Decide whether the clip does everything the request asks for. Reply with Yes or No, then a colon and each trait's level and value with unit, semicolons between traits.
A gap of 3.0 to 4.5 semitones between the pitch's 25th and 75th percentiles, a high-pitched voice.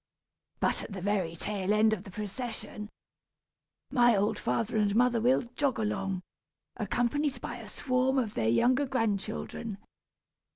Yes: average, 3.8 semitones; high, 220 Hz